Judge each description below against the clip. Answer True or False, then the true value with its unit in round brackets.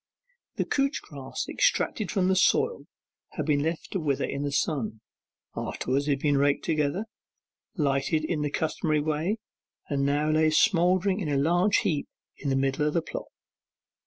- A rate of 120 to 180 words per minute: True (165 wpm)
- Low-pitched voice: False (155 Hz)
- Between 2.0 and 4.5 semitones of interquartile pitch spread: True (3.8 semitones)